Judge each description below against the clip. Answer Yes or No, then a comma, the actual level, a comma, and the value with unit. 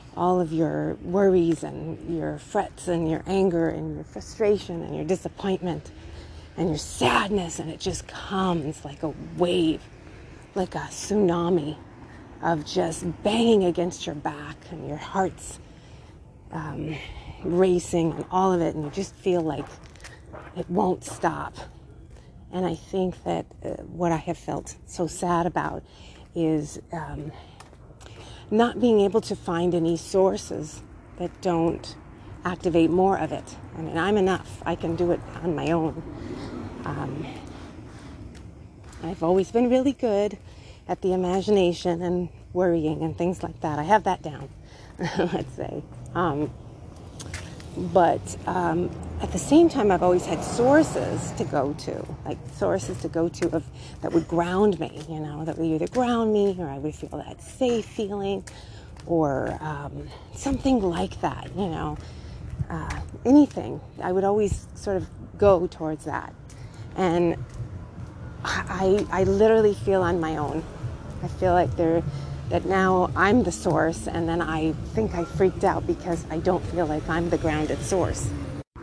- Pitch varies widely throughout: No, average, 3.8 semitones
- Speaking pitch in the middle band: Yes, medium, 170 Hz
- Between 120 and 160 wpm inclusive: Yes, average, 150 wpm